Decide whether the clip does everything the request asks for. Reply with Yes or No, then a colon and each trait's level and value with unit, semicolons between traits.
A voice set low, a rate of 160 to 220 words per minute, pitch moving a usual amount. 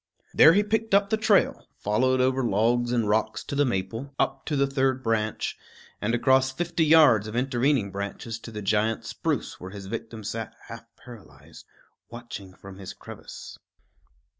Yes: low, 120 Hz; average, 165 wpm; average, 4.2 semitones